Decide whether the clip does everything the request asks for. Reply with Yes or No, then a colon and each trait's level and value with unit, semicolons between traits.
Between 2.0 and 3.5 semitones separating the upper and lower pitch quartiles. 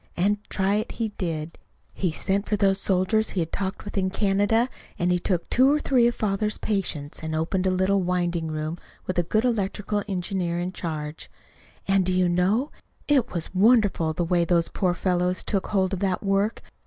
Yes: average, 2.8 semitones